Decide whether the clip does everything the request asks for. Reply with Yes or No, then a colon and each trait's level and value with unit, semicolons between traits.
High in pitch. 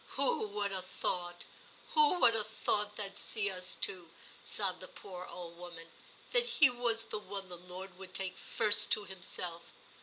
Yes: high, 195 Hz